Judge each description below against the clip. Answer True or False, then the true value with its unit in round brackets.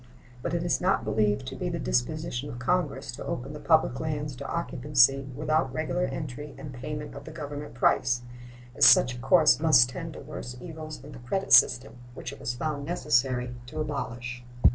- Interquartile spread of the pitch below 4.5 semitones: True (3.9 semitones)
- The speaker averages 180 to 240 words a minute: True (190 wpm)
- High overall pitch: False (140 Hz)